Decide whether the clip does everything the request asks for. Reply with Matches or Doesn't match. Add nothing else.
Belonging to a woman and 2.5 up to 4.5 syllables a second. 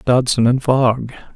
Doesn't match